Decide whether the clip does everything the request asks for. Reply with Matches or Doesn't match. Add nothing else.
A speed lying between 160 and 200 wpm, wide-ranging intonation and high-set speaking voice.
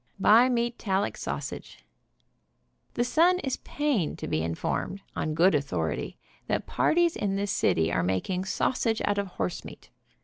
Doesn't match